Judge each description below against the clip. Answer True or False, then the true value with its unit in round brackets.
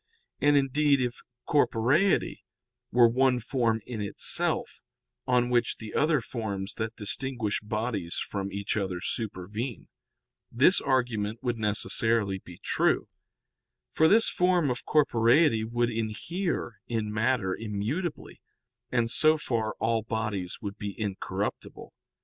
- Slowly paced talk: True (120 wpm)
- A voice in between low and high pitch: False (115 Hz)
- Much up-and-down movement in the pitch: False (3.6 semitones)